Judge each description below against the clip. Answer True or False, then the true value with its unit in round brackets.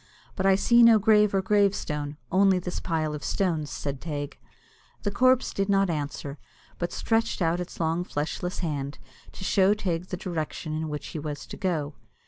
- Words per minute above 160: True (180 wpm)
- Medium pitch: True (175 Hz)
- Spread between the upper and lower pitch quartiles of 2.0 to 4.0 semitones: False (4.4 semitones)